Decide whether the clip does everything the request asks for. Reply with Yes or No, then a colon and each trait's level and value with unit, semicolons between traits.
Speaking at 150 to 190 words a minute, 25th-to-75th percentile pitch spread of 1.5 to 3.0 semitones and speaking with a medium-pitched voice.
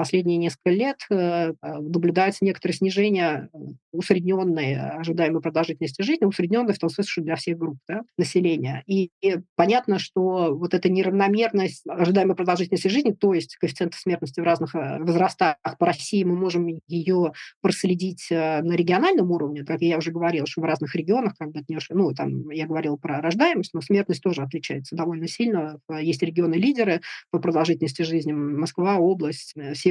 Yes: fast, 160 wpm; narrow, 2.5 semitones; medium, 170 Hz